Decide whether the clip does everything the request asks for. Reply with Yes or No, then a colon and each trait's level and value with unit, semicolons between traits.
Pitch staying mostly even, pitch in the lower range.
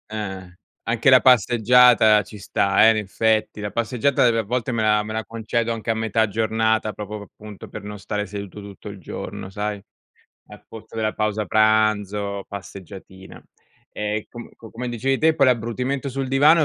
Yes: narrow, 2.2 semitones; low, 110 Hz